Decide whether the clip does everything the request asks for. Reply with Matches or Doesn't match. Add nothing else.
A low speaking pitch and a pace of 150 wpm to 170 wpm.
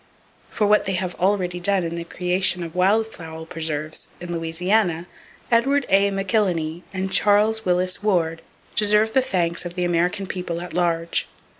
Doesn't match